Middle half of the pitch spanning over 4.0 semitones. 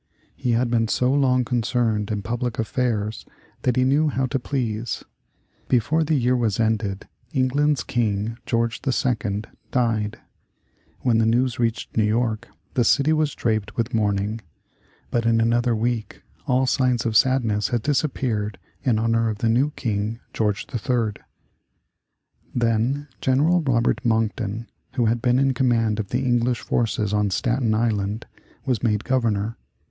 No: average, 2.7 semitones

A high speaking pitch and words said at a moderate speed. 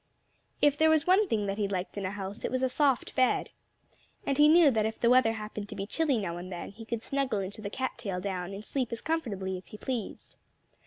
No: high, 220 Hz; fast, 250 wpm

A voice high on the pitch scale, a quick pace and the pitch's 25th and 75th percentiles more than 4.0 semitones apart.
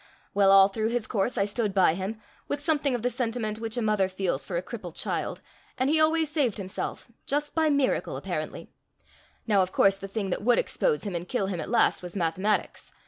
Yes: high, 215 Hz; fast, 210 wpm; average, 4.5 semitones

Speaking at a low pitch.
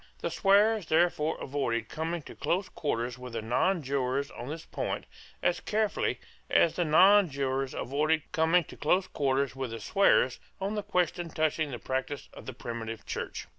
No: medium, 150 Hz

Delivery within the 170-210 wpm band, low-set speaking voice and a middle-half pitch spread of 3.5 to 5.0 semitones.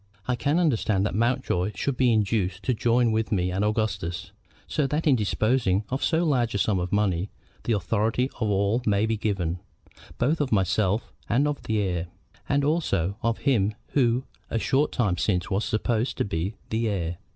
Yes: average, 185 wpm; low, 110 Hz; average, 4.4 semitones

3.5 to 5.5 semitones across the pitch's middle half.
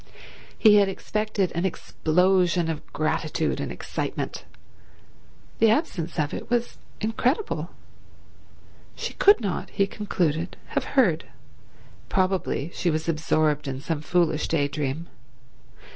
Yes: average, 4.8 semitones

